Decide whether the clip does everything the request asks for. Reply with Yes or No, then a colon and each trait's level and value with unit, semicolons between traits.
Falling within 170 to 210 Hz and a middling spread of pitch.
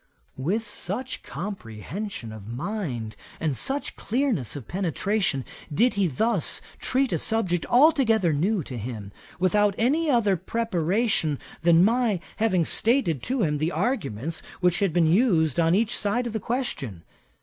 No: high, 190 Hz; wide, 6.6 semitones